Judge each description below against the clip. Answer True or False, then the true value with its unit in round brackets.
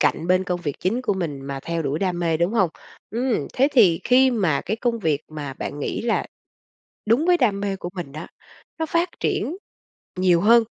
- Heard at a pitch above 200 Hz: False (185 Hz)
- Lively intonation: True (6.5 semitones)